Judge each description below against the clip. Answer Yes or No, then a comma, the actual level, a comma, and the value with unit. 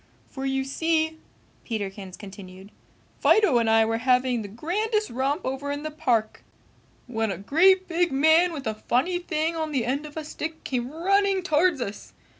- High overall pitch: Yes, very high, 280 Hz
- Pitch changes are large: Yes, wide, 6.0 semitones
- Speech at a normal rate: Yes, average, 175 wpm